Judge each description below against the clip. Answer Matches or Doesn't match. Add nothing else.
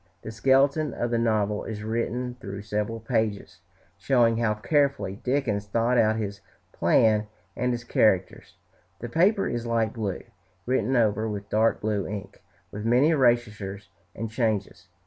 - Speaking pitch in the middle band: Doesn't match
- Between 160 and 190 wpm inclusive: Doesn't match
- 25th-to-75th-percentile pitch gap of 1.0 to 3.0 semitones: Matches